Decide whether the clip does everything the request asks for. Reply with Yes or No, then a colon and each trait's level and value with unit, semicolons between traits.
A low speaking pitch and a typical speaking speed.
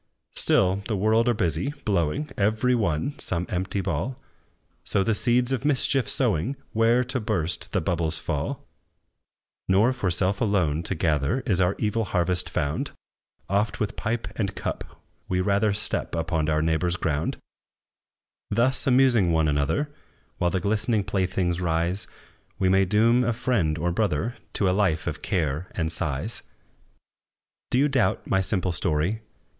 Yes: very low, 95 Hz; average, 150 wpm